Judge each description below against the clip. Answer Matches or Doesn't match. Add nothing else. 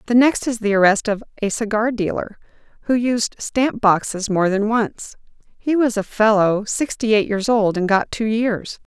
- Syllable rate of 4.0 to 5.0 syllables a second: Matches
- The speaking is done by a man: Doesn't match